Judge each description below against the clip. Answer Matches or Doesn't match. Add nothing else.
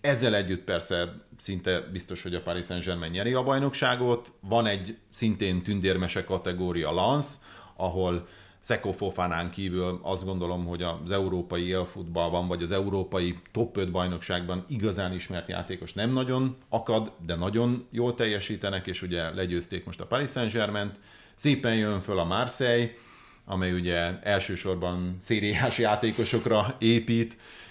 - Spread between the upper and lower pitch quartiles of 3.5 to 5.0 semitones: Matches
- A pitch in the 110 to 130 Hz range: Doesn't match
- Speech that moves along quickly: Doesn't match